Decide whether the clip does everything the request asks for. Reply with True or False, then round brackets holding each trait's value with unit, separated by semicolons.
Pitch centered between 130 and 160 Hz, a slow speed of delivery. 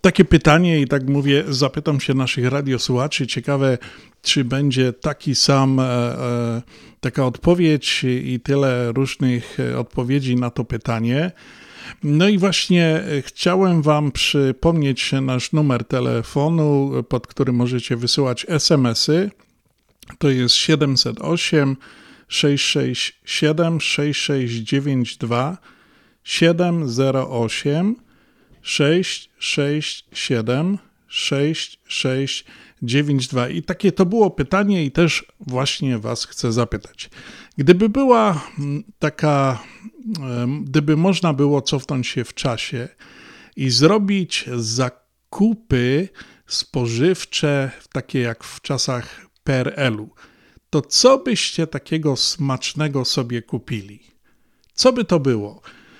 True (140 Hz; 100 wpm)